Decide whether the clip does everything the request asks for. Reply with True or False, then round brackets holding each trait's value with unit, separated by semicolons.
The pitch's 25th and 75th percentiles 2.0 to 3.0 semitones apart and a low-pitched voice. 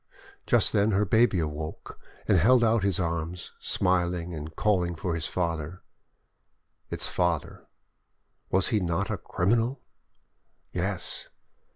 False (3.8 semitones; 90 Hz)